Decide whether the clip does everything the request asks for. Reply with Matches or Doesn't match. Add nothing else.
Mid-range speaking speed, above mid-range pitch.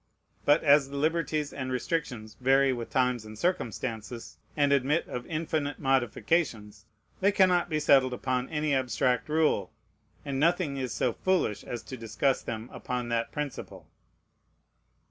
Doesn't match